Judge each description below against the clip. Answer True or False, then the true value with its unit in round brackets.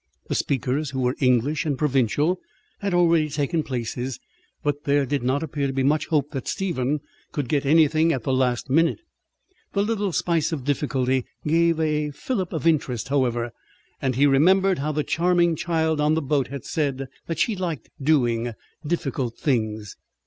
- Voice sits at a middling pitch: True (145 Hz)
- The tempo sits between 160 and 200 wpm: True (170 wpm)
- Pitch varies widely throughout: False (3.6 semitones)